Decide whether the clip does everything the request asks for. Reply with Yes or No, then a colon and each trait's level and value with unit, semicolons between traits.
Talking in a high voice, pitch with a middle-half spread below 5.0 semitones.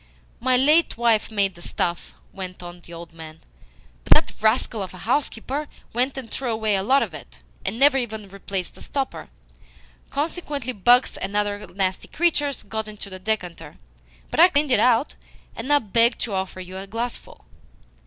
No: high, 220 Hz; average, 5.3 semitones